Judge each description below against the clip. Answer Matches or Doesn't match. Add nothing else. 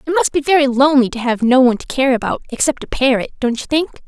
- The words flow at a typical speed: Doesn't match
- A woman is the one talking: Matches